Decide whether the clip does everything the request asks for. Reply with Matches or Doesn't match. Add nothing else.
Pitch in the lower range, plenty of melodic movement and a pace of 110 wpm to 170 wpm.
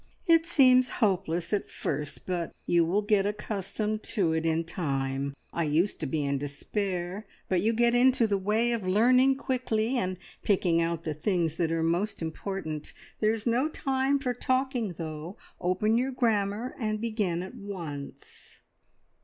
Doesn't match